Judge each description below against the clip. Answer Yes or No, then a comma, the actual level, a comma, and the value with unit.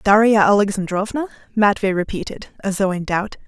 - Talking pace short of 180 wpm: Yes, average, 140 wpm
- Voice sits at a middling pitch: No, high, 200 Hz